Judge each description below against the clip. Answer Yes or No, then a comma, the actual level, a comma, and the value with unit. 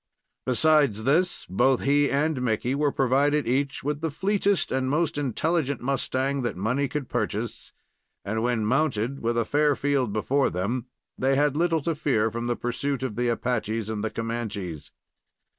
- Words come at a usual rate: Yes, average, 165 wpm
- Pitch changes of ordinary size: Yes, average, 3.8 semitones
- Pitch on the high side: No, low, 135 Hz